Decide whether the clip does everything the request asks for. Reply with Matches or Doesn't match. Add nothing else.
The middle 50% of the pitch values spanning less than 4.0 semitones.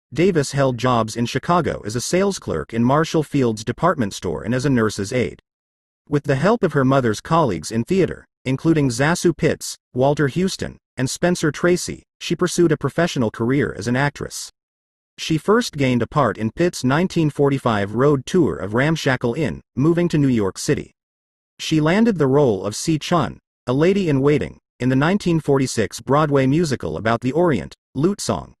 Doesn't match